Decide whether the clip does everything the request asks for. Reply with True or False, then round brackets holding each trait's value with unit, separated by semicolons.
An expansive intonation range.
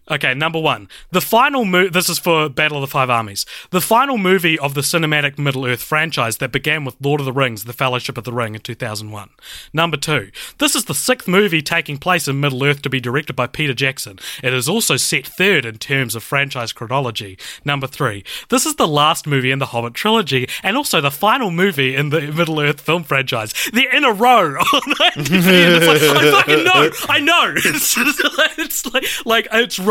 True (6.9 semitones)